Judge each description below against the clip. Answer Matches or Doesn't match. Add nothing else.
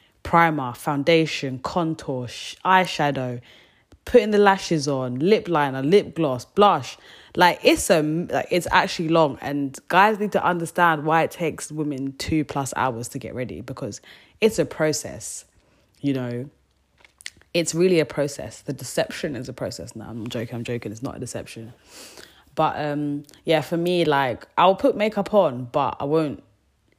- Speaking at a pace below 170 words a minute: Matches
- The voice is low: Doesn't match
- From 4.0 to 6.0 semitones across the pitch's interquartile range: Matches